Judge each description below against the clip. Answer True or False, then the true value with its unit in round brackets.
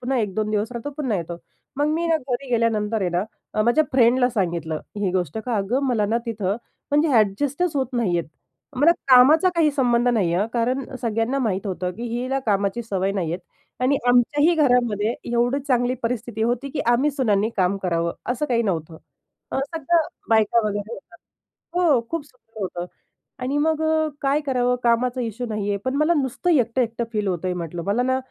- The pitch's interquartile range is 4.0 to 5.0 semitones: True (4.6 semitones)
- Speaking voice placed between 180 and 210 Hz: False (235 Hz)